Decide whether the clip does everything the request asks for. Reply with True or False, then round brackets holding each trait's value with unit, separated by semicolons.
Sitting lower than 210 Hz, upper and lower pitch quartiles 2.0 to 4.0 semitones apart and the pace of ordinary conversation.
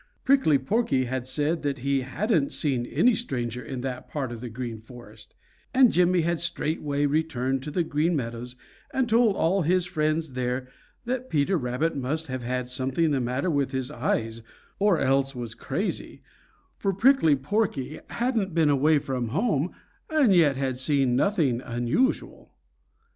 False (140 Hz; 5.2 semitones; 160 wpm)